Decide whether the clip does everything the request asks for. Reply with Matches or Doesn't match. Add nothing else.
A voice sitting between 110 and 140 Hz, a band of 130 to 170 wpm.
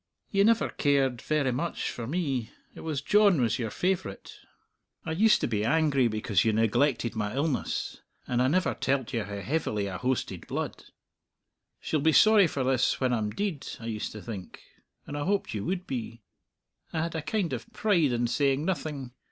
Doesn't match